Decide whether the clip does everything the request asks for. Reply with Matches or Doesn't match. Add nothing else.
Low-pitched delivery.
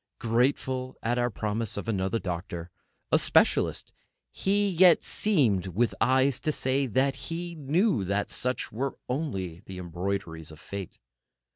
Matches